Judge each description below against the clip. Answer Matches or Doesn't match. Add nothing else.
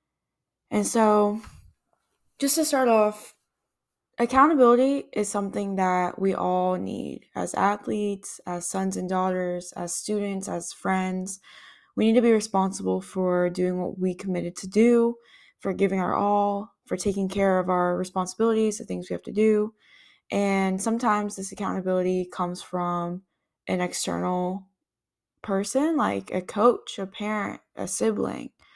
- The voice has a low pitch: Doesn't match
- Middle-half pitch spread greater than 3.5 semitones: Doesn't match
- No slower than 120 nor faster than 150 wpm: Matches